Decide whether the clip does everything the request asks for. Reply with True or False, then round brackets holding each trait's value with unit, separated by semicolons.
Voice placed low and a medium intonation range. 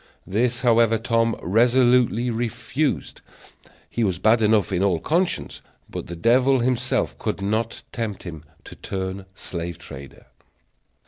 True (115 Hz; 4.2 semitones)